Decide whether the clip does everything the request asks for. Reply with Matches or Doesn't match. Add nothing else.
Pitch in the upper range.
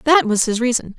Matches